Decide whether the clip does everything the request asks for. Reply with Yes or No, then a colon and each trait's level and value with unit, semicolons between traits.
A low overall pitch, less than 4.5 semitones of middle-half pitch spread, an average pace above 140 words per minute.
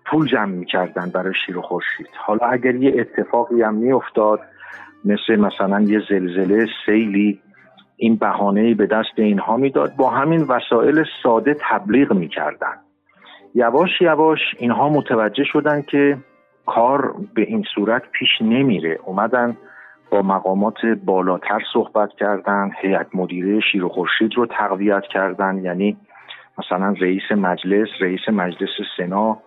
No: low, 105 Hz; average, 3.6 semitones; average, 125 wpm